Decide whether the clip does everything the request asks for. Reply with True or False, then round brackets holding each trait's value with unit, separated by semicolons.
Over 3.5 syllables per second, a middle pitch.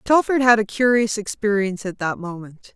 False (5.3 syllables/s; 210 Hz)